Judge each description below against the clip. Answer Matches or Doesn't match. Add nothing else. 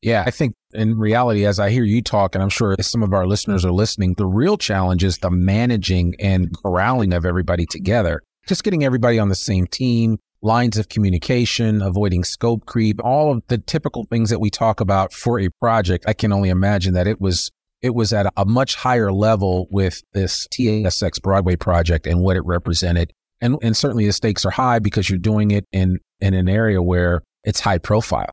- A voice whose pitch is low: Matches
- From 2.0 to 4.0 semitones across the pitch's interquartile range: Matches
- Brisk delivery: Matches